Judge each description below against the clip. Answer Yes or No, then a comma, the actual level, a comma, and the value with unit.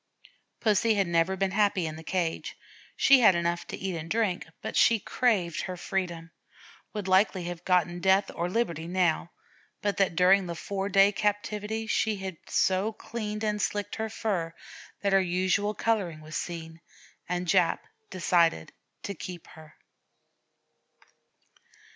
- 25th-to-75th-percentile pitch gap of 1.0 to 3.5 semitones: Yes, average, 3.2 semitones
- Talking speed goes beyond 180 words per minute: No, average, 150 wpm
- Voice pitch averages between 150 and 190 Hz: Yes, medium, 185 Hz